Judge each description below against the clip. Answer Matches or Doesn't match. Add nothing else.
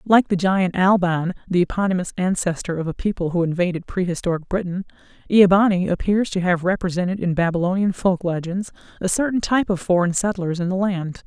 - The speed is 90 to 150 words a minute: Doesn't match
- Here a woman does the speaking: Matches